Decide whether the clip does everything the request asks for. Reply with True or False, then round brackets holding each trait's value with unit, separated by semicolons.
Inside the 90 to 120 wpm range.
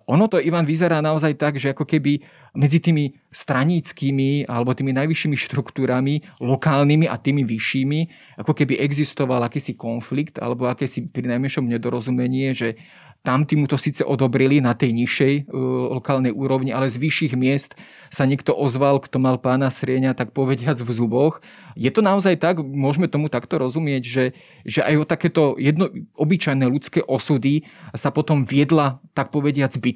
False (160 wpm)